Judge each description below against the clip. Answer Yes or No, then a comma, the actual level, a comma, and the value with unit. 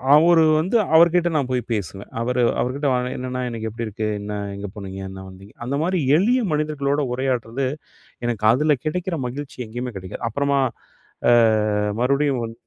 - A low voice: Yes, low, 125 Hz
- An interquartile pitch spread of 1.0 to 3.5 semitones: No, average, 4.9 semitones